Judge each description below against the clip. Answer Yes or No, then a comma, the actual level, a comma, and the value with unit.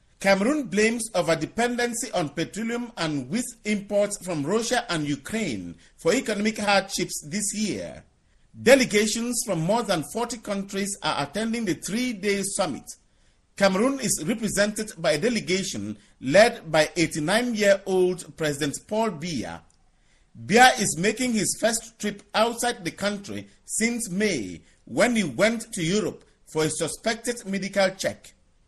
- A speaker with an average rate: No, slow, 130 wpm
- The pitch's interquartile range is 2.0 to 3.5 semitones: No, wide, 5.4 semitones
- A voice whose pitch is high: Yes, high, 205 Hz